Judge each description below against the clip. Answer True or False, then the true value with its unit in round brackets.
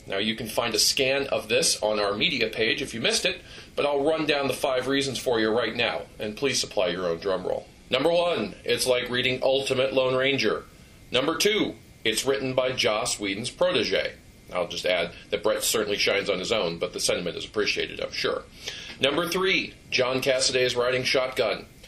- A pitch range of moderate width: False (6.0 semitones)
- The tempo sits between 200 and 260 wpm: True (205 wpm)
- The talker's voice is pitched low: True (130 Hz)